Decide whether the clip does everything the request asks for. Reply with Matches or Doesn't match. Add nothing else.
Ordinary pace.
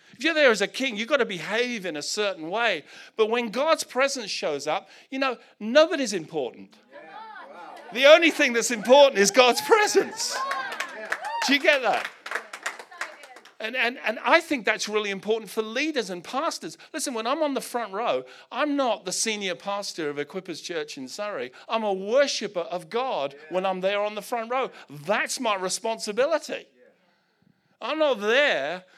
Matches